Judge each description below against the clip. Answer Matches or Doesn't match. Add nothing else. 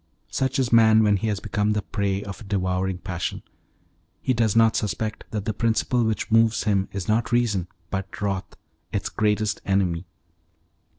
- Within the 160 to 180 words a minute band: Matches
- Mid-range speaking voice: Doesn't match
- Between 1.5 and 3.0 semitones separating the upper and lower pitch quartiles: Matches